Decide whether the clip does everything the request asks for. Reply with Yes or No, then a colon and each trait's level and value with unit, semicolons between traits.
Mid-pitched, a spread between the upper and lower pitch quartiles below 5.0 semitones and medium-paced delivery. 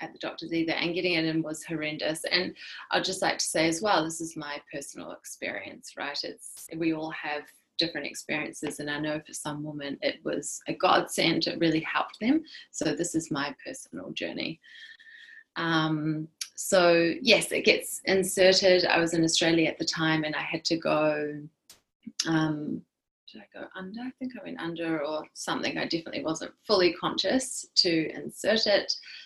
Yes: medium, 165 Hz; average, 3.9 semitones; average, 180 wpm